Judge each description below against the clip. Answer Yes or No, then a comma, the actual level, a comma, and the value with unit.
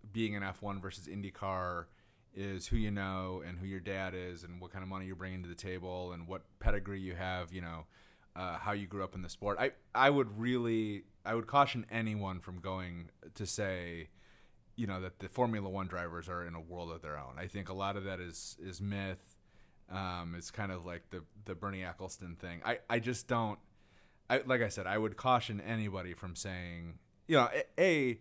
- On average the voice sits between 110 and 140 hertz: No, very low, 95 Hz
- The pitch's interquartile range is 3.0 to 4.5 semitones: No, narrow, 2.5 semitones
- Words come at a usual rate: No, fast, 215 wpm